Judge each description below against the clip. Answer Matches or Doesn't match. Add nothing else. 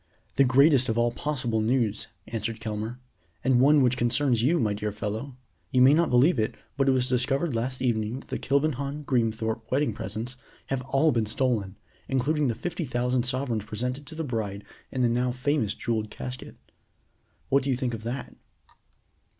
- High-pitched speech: Doesn't match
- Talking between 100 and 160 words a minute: Doesn't match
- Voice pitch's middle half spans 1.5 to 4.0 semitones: Matches